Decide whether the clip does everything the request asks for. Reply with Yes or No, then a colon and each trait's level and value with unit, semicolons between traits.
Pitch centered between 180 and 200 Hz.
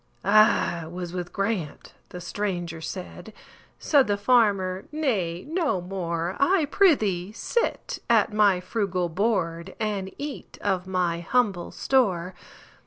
Yes: high, 190 Hz